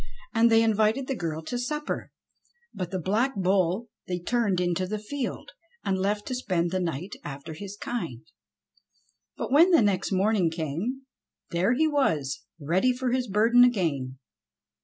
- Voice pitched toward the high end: Yes, high, 200 Hz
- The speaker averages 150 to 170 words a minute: Yes, average, 160 wpm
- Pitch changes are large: Yes, wide, 5.9 semitones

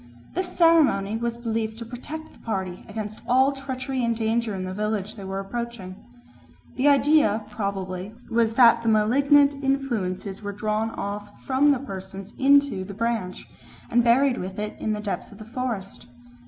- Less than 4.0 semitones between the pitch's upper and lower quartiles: No, average, 4.4 semitones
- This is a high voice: Yes, high, 225 Hz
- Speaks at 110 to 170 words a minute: Yes, average, 165 wpm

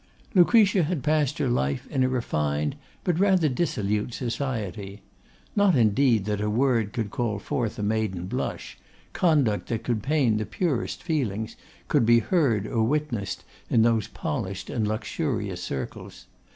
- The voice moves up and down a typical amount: No, wide, 5.7 semitones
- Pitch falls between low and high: No, low, 115 Hz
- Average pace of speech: Yes, average, 150 wpm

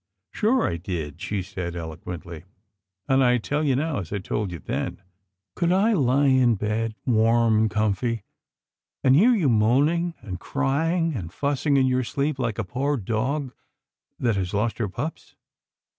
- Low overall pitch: Yes, low, 115 Hz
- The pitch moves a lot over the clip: Yes, wide, 6.5 semitones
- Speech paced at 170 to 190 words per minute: Yes, average, 180 wpm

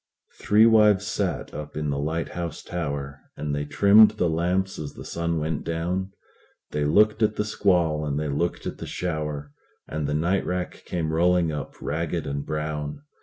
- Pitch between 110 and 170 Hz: No, very low, 80 Hz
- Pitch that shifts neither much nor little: Yes, average, 3.4 semitones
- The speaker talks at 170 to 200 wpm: Yes, average, 175 wpm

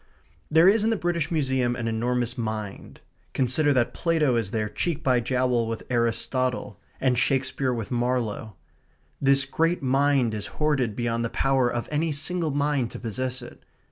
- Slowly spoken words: No, average, 165 wpm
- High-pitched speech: No, low, 130 Hz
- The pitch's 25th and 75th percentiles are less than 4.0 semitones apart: Yes, average, 3.5 semitones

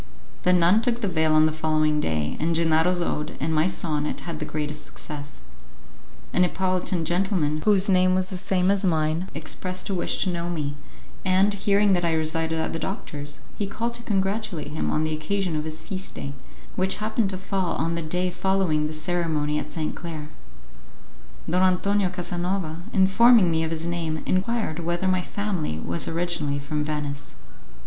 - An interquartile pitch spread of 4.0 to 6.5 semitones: No, average, 3.5 semitones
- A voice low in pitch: No, medium, 170 Hz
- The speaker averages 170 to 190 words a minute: Yes, average, 180 wpm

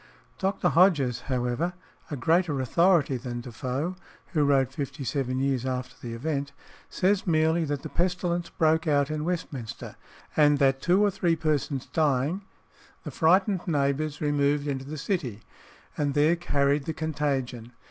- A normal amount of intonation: Yes, average, 3.7 semitones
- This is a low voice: No, medium, 145 Hz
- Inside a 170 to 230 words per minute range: No, average, 145 wpm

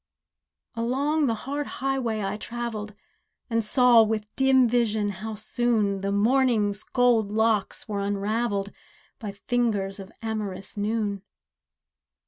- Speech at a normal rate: No, slow, 115 wpm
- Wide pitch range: No, average, 2.8 semitones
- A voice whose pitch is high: Yes, high, 220 Hz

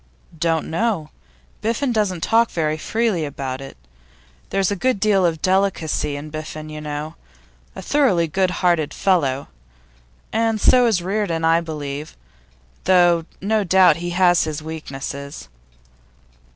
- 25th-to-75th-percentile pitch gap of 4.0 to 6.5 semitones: Yes, average, 4.3 semitones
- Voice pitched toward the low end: No, medium, 170 Hz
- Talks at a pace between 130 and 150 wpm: Yes, slow, 135 wpm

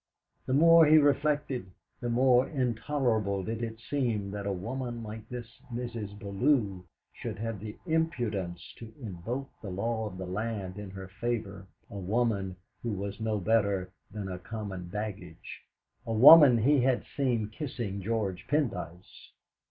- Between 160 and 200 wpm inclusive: No, average, 150 wpm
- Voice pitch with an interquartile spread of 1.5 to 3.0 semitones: No, average, 4.0 semitones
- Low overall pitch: Yes, low, 110 Hz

